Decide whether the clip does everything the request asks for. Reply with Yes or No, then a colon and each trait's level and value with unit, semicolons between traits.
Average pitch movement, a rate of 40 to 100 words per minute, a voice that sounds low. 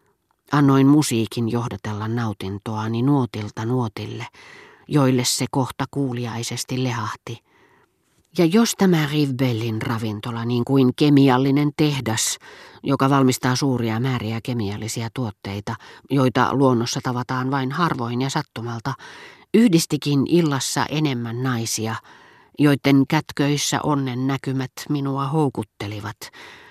Yes: average, 3.4 semitones; slow, 95 wpm; low, 130 Hz